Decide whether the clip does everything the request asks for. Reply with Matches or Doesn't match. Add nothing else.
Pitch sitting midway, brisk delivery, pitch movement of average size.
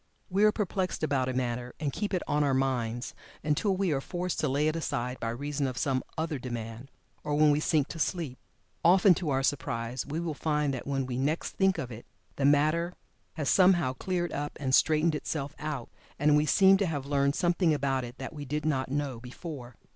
Matches